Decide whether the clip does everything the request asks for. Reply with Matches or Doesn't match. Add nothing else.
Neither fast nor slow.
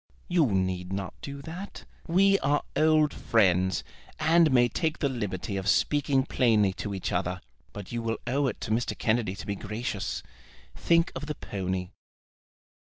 Matches